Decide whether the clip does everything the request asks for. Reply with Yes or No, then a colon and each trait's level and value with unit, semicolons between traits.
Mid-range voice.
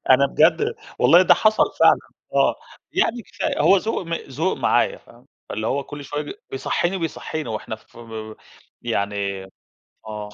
Yes: medium, 145 Hz